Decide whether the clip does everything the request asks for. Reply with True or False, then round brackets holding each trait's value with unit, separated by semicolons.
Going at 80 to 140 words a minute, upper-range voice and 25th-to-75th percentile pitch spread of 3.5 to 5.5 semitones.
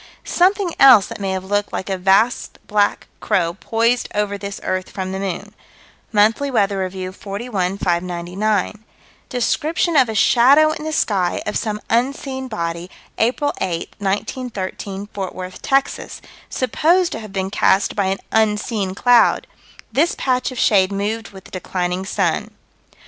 False (150 wpm; 205 Hz; 4.5 semitones)